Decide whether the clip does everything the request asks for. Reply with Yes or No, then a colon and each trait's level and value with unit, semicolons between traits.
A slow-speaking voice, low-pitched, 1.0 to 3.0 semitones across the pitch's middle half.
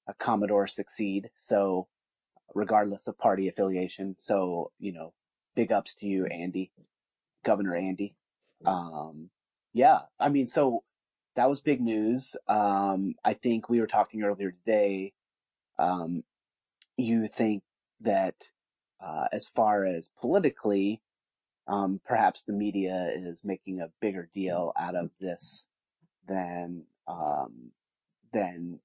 Yes: slow, 125 wpm; low, 100 Hz; average, 2.7 semitones